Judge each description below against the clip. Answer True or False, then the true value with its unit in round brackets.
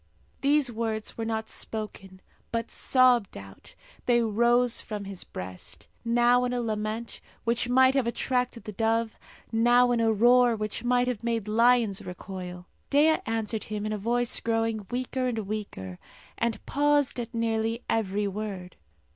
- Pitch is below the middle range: False (230 Hz)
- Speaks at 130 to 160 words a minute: True (155 wpm)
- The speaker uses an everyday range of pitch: False (2.3 semitones)